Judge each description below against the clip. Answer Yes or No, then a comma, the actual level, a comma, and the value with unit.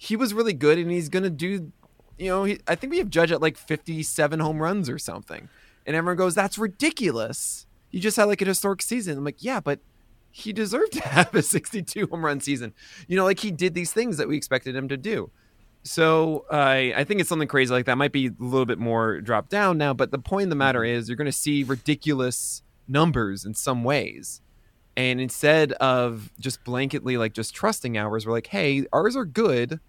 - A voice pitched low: No, medium, 150 Hz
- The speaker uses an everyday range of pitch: No, wide, 6.6 semitones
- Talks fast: Yes, fast, 220 wpm